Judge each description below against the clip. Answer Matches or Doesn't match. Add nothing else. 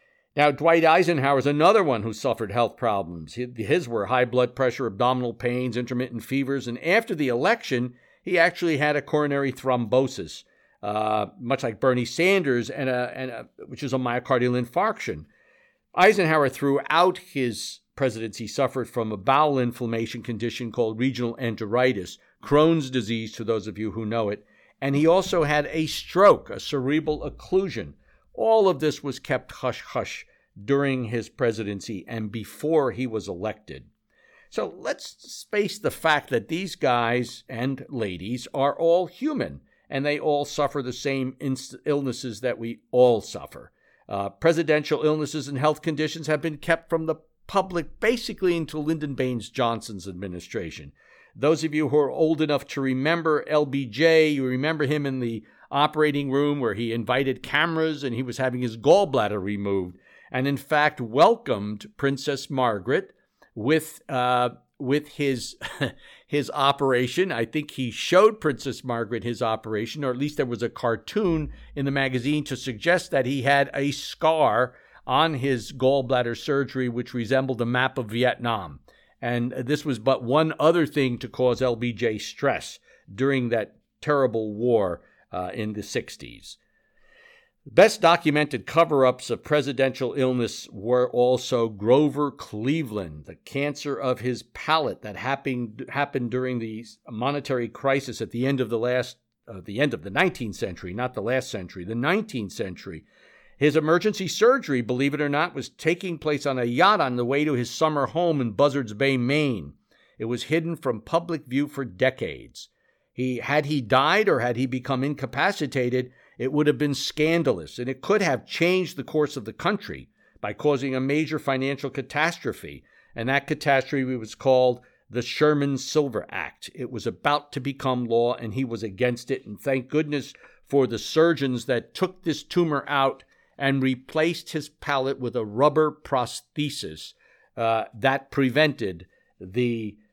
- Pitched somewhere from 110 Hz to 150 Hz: Matches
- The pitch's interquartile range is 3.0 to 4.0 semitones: Matches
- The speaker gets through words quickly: Doesn't match